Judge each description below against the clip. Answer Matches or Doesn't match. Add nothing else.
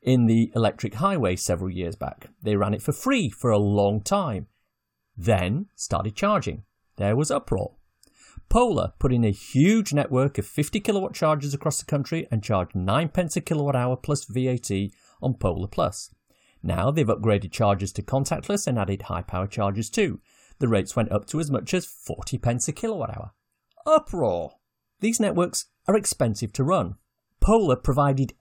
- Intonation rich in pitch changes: Matches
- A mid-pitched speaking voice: Doesn't match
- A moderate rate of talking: Matches